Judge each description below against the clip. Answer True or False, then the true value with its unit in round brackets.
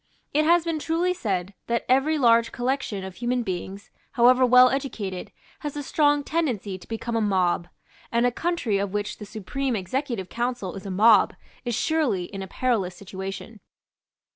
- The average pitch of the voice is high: True (235 Hz)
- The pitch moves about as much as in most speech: False (5.8 semitones)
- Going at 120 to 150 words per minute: False (170 wpm)